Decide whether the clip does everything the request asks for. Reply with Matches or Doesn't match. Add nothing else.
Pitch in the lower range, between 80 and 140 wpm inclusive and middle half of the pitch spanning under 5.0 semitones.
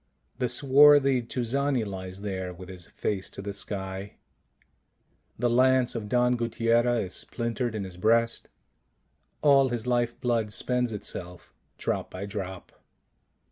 Matches